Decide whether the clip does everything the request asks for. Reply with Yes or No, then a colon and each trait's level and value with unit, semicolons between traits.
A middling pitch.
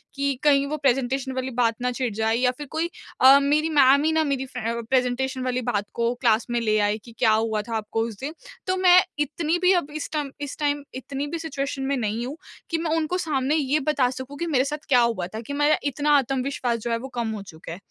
No: very high, 265 Hz